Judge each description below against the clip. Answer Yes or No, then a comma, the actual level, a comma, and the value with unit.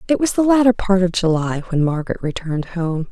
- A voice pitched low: No, high, 190 Hz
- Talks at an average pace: No, fast, 210 wpm